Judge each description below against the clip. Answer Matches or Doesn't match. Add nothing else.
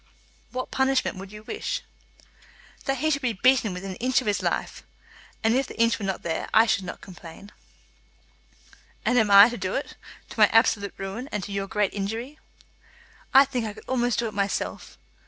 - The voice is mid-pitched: Doesn't match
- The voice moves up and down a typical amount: Matches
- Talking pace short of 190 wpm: Doesn't match